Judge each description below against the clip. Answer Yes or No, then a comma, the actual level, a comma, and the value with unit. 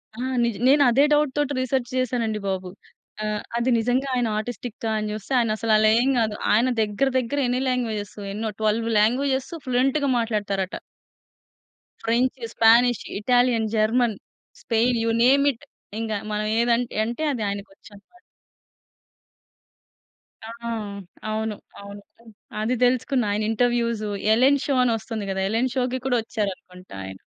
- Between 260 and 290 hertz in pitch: No, high, 230 Hz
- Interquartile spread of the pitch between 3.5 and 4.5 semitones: No, average, 2.8 semitones